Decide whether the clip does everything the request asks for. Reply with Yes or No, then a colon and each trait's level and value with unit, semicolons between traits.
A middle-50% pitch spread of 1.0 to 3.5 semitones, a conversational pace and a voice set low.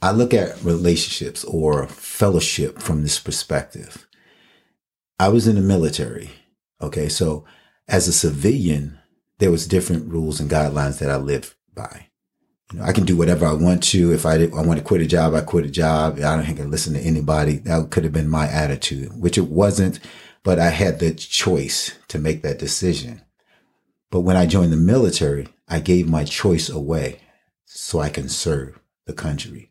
Yes: narrow, 2.6 semitones; average, 190 wpm; very low, 80 Hz